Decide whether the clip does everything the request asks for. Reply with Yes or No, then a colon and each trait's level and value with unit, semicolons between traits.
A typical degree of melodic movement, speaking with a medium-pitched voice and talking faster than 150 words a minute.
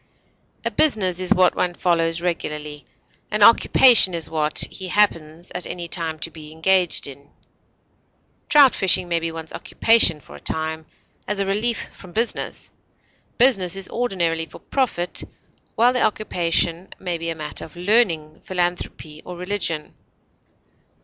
No: average, 3.5 semitones; medium, 175 Hz; average, 145 wpm